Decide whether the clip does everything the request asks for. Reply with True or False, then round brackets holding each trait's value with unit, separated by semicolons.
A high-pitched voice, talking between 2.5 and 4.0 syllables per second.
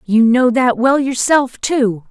True (245 Hz; 3.5 syllables/s)